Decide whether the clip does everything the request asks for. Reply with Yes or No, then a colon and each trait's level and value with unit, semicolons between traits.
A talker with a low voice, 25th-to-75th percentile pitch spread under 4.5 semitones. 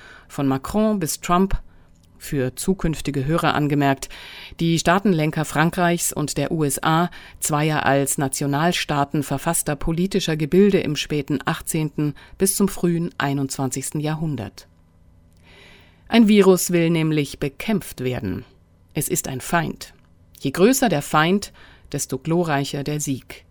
No: medium, 150 Hz; average, 4.0 semitones